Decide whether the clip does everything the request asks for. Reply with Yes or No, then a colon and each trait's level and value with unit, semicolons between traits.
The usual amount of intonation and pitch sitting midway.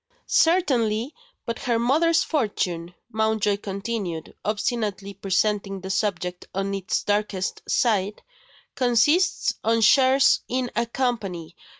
No: average, 3.8 semitones; high, 215 Hz